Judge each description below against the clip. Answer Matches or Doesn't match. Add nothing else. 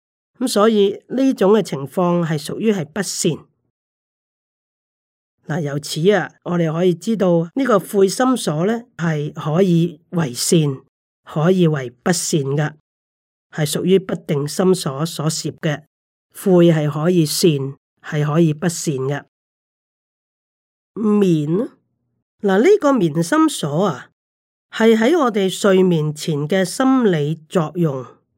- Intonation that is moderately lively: Matches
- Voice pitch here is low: Doesn't match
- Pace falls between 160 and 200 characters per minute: Matches